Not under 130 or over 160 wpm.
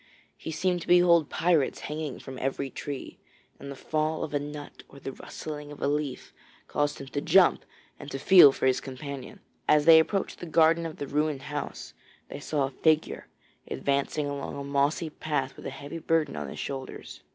No: average, 195 wpm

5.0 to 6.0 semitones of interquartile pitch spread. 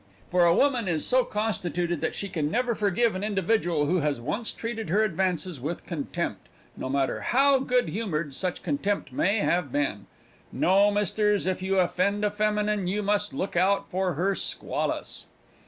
No: average, 3.6 semitones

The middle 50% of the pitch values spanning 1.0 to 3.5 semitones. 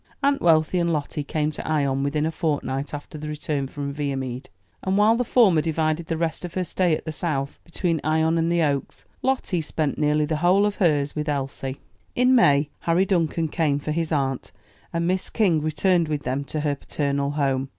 Yes: average, 3.1 semitones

